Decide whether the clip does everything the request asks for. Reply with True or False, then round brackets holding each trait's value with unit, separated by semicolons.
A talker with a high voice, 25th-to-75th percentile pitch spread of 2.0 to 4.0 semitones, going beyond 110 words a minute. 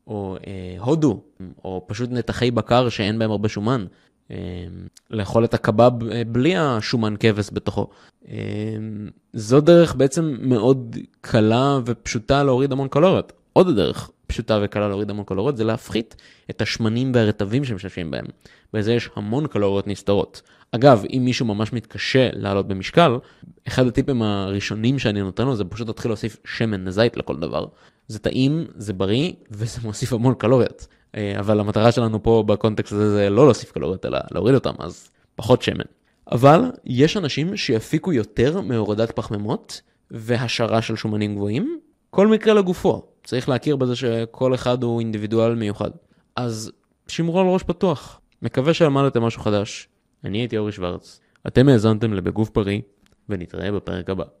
False (115 Hz; 3.6 semitones; 150 wpm)